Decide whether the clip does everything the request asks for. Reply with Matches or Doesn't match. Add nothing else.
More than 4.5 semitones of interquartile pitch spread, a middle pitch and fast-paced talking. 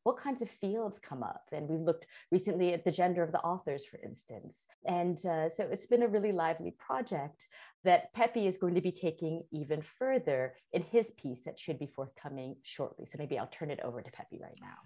Matches